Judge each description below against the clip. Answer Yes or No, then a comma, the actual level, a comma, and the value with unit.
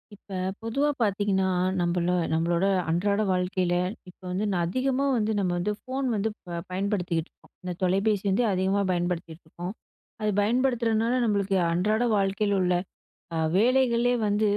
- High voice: Yes, high, 200 Hz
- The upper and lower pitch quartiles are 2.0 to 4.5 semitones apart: Yes, average, 3.5 semitones